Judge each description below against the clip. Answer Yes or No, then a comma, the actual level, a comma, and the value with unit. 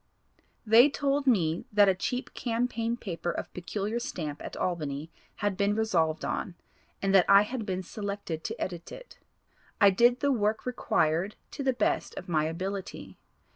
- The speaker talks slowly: No, average, 165 wpm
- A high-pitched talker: Yes, high, 200 Hz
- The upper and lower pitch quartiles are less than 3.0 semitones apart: No, average, 5.2 semitones